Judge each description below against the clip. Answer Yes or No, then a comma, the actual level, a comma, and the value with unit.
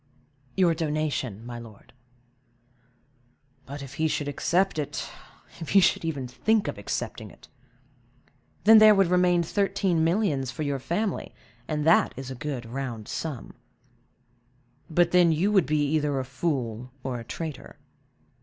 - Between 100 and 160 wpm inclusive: Yes, average, 145 wpm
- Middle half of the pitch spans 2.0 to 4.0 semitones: No, average, 5.0 semitones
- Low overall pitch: No, medium, 155 Hz